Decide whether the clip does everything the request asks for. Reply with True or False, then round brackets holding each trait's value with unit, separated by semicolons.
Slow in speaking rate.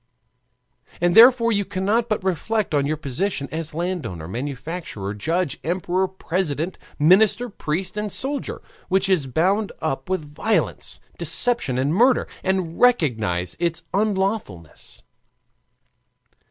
True (115 wpm)